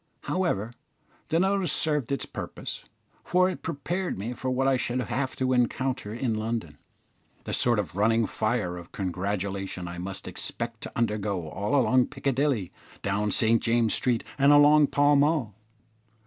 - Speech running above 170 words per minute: No, average, 155 wpm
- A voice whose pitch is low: Yes, low, 120 Hz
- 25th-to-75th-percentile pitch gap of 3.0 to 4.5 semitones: No, average, 5.2 semitones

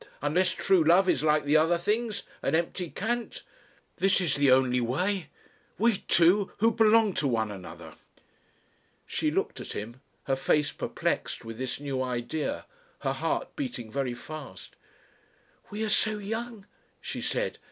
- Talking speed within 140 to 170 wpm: Yes, average, 150 wpm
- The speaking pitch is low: No, medium, 165 Hz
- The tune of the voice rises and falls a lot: Yes, wide, 7.7 semitones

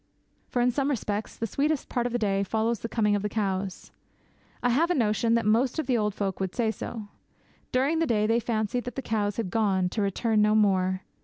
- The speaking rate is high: Yes, fast, 230 wpm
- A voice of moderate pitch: No, high, 220 Hz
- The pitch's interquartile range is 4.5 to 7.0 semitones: No, average, 3.0 semitones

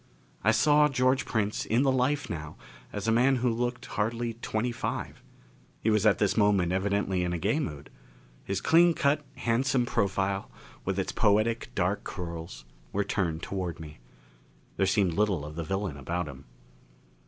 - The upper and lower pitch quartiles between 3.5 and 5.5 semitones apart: Yes, average, 5.1 semitones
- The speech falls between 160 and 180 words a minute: Yes, average, 165 wpm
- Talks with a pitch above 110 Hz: No, low, 105 Hz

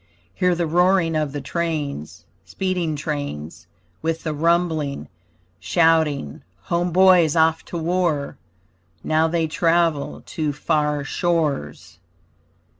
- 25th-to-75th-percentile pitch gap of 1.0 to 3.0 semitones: Yes, average, 2.7 semitones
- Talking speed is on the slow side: Yes, slow, 110 wpm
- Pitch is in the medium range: Yes, medium, 160 Hz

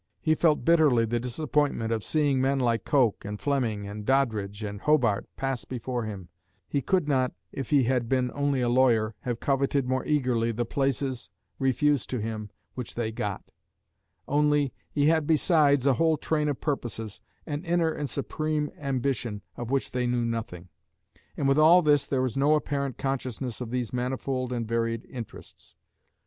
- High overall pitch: No, low, 130 Hz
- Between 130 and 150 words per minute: No, average, 170 wpm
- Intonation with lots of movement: No, average, 3.8 semitones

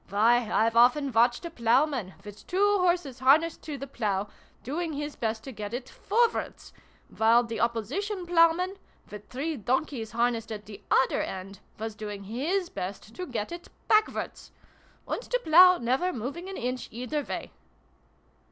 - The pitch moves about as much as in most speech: No, wide, 6.9 semitones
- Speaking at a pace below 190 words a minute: Yes, average, 160 wpm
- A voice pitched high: Yes, very high, 250 Hz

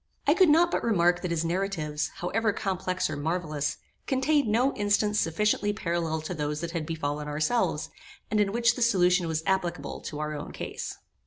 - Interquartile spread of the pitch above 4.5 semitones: Yes, average, 4.9 semitones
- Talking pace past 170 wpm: Yes, average, 180 wpm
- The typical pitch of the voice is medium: Yes, medium, 180 Hz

